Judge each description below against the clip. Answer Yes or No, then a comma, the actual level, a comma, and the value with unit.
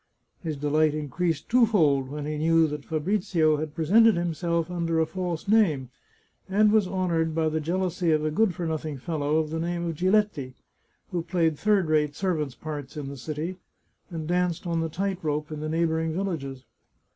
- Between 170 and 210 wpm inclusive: Yes, average, 180 wpm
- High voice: No, medium, 160 Hz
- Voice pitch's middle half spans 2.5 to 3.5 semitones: Yes, average, 2.8 semitones